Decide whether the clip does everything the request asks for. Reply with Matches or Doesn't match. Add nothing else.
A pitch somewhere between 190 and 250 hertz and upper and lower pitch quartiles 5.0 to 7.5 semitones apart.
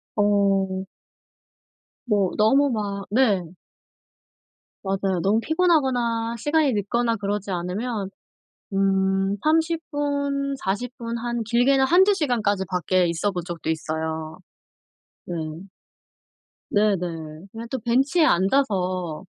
Matches